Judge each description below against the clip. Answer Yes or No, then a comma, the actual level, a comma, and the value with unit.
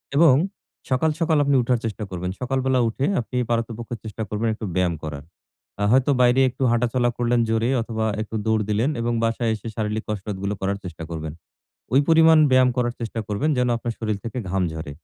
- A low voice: Yes, low, 115 Hz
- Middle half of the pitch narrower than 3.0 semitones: No, average, 3.3 semitones